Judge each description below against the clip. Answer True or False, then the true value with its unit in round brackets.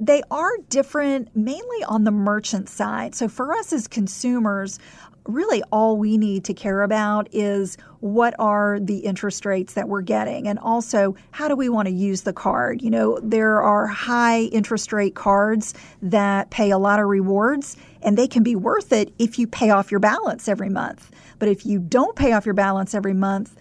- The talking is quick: False (195 wpm)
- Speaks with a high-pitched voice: True (210 Hz)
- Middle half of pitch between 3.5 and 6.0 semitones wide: False (2.6 semitones)